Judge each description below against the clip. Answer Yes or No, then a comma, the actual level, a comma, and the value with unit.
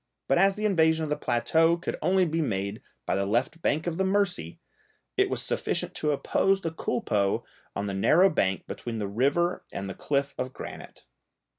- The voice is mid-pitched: Yes, medium, 150 Hz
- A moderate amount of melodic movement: No, wide, 8.5 semitones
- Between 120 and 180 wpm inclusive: No, average, 190 wpm